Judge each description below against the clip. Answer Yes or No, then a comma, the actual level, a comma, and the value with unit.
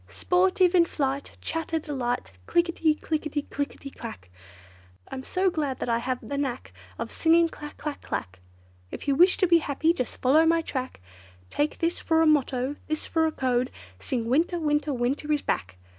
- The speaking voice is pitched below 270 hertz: No, very high, 295 Hz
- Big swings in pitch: No, average, 3.9 semitones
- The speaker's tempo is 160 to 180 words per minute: No, average, 190 wpm